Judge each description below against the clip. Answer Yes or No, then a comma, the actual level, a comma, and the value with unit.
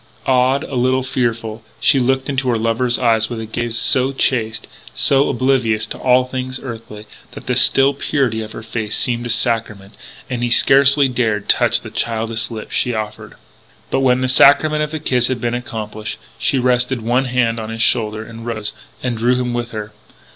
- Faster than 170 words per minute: Yes, average, 190 wpm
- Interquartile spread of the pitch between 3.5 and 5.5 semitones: No, narrow, 2.5 semitones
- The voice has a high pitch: No, low, 120 Hz